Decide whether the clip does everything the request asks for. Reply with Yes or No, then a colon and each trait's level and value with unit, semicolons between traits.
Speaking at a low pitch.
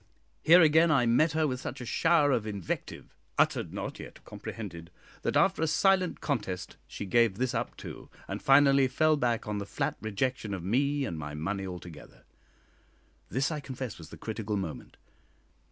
Yes: low, 120 Hz